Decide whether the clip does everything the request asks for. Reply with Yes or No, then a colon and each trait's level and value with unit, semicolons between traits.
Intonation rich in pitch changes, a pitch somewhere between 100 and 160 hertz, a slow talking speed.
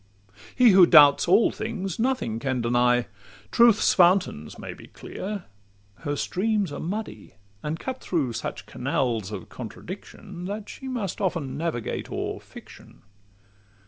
No: wide, 8.7 semitones; medium, 170 Hz; slow, 130 wpm